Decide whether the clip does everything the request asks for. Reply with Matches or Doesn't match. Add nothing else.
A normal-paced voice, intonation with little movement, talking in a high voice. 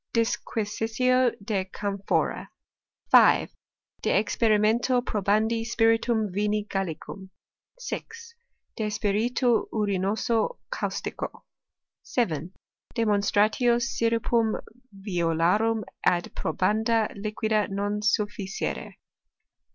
Doesn't match